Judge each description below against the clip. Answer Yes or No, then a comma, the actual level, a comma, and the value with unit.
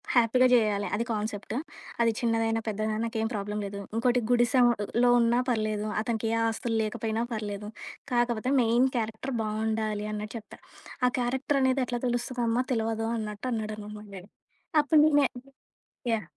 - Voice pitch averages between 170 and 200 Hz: No, high, 225 Hz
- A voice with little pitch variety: Yes, narrow, 2.1 semitones